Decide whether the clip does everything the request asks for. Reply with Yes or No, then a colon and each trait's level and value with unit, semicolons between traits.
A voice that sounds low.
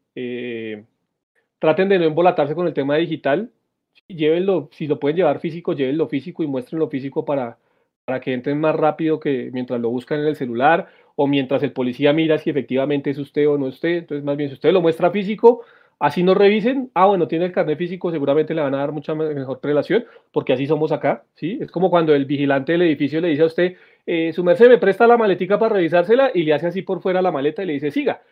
No: medium, 155 Hz